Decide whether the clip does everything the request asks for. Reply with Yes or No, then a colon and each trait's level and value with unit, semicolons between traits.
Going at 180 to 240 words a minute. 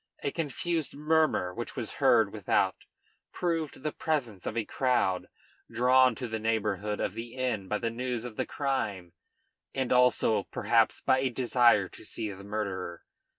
No: average, 160 wpm